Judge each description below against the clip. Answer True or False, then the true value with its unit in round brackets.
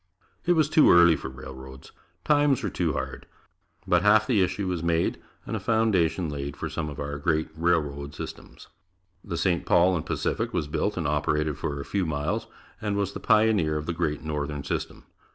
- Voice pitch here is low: True (80 Hz)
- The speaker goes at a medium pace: True (190 wpm)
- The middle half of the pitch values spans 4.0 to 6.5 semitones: True (5.3 semitones)